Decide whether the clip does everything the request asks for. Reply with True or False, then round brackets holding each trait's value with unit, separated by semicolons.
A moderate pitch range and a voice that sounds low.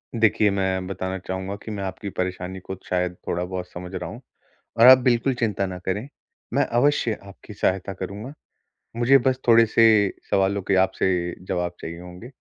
True (3.7 semitones; 95 Hz)